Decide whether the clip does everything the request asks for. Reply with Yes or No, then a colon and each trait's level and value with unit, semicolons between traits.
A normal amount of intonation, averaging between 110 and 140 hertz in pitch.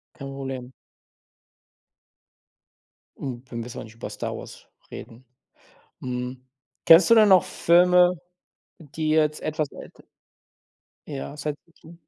No: average, 4.7 semitones; medium, 150 Hz